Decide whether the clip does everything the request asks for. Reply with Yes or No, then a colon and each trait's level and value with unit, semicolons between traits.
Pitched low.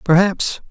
No: medium, 180 Hz